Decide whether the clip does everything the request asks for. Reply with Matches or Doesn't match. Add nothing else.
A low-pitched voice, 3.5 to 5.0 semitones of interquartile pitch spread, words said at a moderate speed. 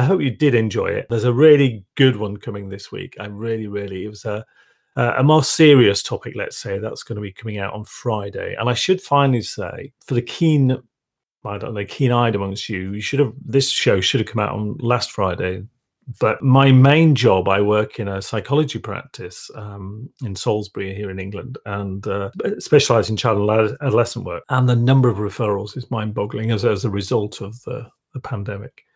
Doesn't match